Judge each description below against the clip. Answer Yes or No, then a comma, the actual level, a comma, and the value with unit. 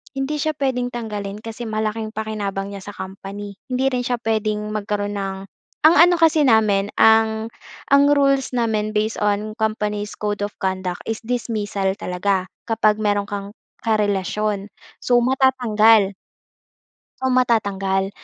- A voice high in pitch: Yes, high, 215 Hz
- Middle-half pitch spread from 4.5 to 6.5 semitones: No, average, 2.8 semitones